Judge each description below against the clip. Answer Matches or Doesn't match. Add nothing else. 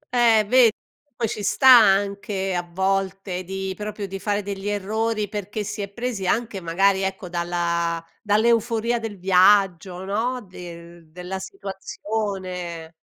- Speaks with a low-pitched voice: Doesn't match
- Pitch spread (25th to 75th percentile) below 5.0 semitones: Matches